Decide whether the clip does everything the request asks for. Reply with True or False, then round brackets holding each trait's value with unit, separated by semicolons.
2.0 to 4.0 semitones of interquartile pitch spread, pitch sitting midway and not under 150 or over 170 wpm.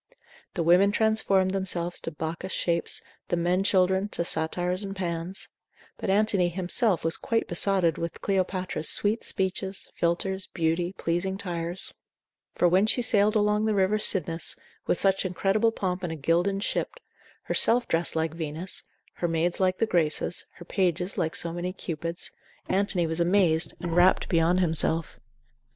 True (2.5 semitones; 180 Hz; 155 wpm)